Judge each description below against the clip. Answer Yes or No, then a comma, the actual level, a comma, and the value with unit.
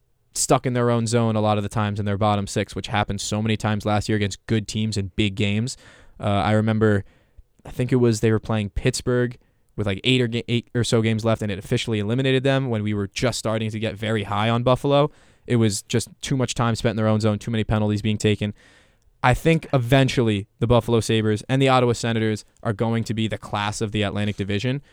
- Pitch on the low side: Yes, low, 110 Hz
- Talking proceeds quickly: Yes, fast, 240 wpm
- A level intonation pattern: Yes, narrow, 2.3 semitones